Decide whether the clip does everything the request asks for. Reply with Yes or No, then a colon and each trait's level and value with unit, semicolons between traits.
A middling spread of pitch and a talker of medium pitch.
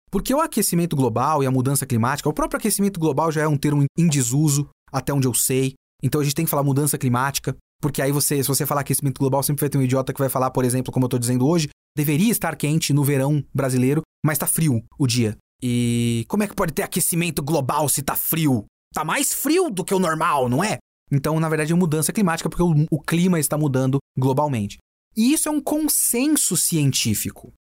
Yes: average, 4.1 semitones; medium, 145 Hz